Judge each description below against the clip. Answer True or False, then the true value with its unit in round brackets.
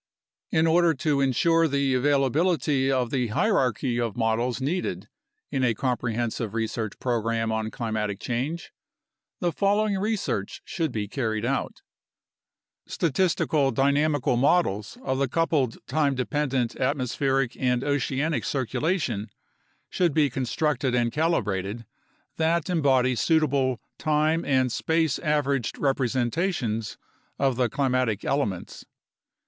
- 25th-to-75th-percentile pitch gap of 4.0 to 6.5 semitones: True (4.5 semitones)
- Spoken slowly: True (115 wpm)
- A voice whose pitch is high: False (135 Hz)